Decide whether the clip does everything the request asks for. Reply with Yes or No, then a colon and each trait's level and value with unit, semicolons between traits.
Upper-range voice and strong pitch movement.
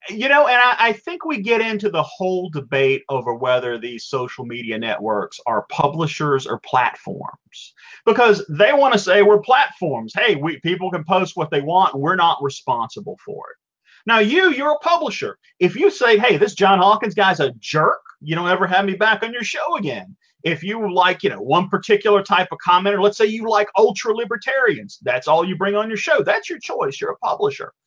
Yes: high, 200 Hz; wide, 5.8 semitones